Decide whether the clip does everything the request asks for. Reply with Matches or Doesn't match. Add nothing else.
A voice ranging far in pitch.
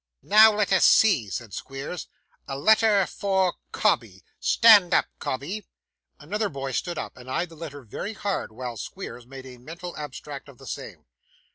Matches